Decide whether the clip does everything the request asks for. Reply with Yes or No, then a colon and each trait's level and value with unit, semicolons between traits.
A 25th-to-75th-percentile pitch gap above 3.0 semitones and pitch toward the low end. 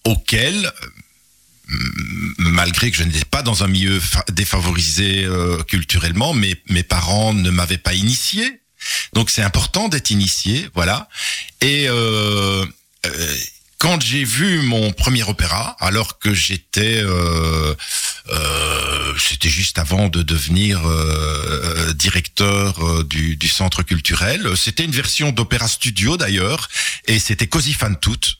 Yes: average, 4.8 semitones; very low, 95 Hz